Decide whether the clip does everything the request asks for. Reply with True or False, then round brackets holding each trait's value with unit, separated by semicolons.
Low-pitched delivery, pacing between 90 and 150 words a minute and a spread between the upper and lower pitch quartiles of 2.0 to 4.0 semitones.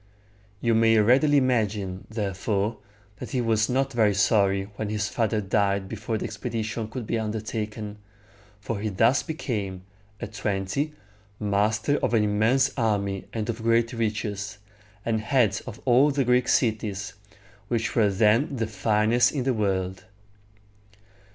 True (110 Hz; 145 wpm; 2.4 semitones)